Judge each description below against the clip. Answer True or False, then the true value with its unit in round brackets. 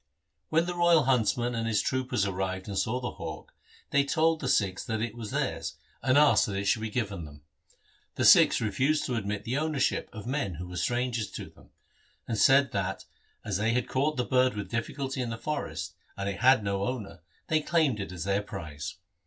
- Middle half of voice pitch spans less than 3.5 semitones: False (5.0 semitones)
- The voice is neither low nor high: False (115 Hz)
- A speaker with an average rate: False (210 wpm)